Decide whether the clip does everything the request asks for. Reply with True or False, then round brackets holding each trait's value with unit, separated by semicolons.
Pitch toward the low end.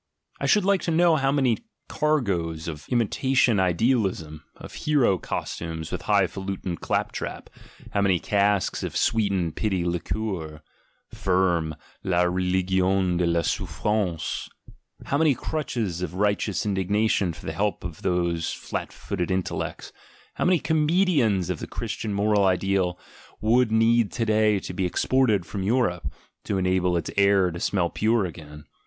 True (95 Hz)